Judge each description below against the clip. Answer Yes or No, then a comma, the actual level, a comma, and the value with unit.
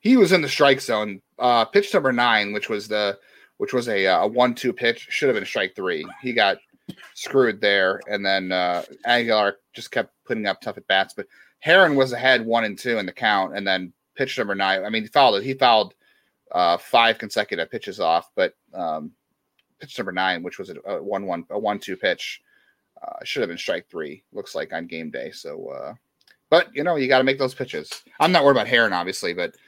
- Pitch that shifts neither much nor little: No, wide, 6.2 semitones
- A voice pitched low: Yes, low, 120 Hz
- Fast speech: Yes, fast, 225 wpm